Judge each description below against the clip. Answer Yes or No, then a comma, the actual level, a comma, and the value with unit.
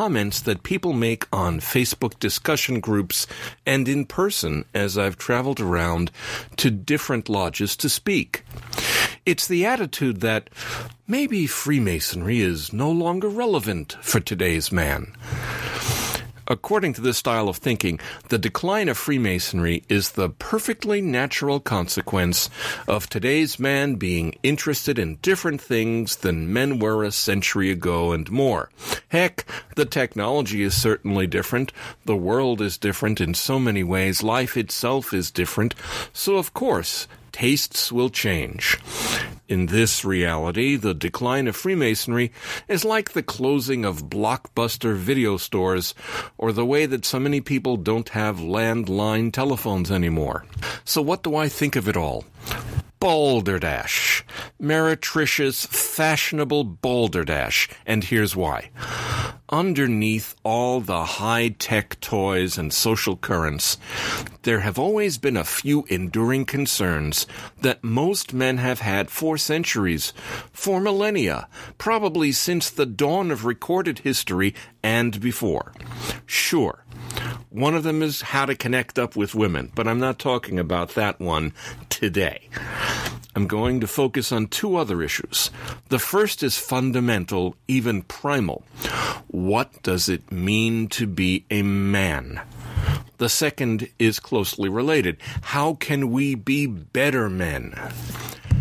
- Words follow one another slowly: Yes, slow, 130 wpm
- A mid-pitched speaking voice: No, low, 115 Hz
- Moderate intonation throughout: No, wide, 5.8 semitones